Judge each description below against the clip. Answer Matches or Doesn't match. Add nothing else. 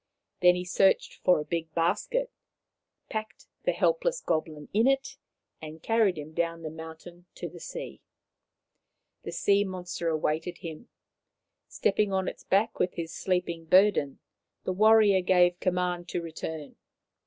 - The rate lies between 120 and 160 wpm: Matches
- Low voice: Doesn't match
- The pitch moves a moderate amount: Matches